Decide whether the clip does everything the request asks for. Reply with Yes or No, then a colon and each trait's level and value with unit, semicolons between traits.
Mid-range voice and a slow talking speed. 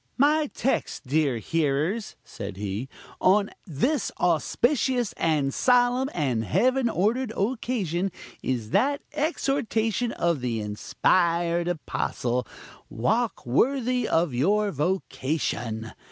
Yes: medium, 175 Hz; slow, 100 wpm